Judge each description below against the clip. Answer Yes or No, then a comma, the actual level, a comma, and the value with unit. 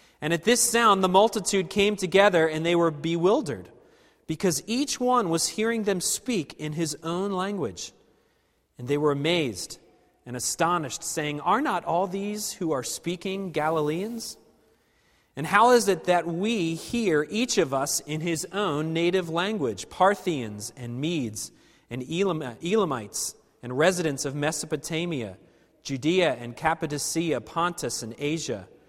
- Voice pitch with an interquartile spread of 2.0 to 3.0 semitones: No, average, 4.5 semitones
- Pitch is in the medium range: Yes, medium, 165 Hz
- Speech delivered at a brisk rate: No, average, 145 wpm